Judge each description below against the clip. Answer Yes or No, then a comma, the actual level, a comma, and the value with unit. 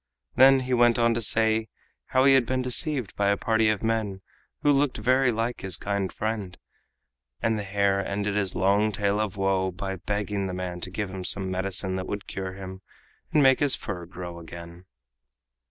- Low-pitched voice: Yes, low, 100 Hz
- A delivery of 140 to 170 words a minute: No, average, 195 wpm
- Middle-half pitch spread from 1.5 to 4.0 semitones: Yes, average, 3.4 semitones